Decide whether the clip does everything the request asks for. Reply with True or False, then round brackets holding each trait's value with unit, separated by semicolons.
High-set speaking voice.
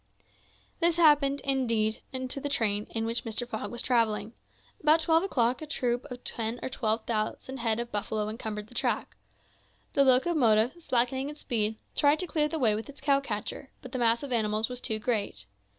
True (245 Hz)